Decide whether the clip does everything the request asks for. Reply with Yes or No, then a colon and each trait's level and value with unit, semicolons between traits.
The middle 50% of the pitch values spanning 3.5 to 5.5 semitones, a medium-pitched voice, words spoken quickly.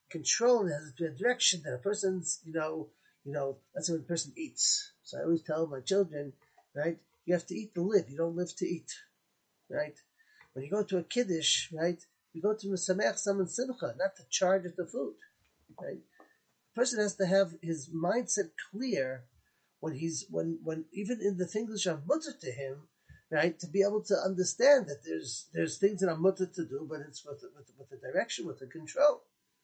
Yes: average, 4.3 semitones; medium, 180 Hz; fast, 210 wpm